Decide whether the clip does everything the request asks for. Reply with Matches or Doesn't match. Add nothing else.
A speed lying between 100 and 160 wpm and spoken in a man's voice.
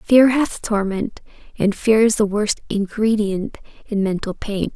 Doesn't match